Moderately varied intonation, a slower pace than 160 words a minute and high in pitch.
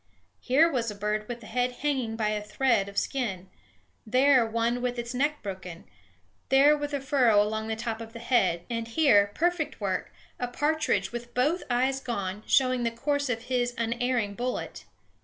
No: average, 3.4 semitones; average, 175 wpm; high, 240 Hz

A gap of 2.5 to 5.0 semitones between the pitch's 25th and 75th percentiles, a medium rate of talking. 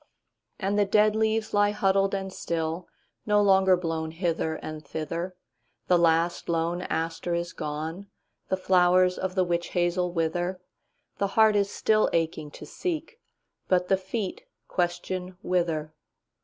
No: average, 2.8 semitones; slow, 125 wpm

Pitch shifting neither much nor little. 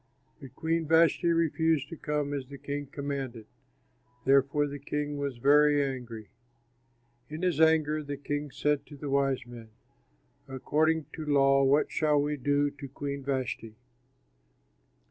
No: narrow, 1.5 semitones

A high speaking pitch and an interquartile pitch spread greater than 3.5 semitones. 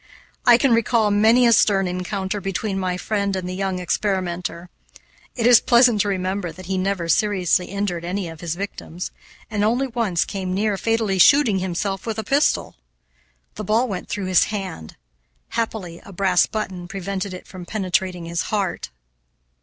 No: high, 195 Hz; average, 2.8 semitones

